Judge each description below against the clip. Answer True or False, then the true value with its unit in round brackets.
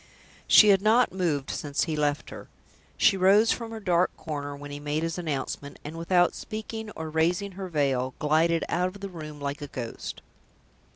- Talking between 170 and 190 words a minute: True (185 wpm)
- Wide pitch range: False (4.7 semitones)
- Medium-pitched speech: True (165 Hz)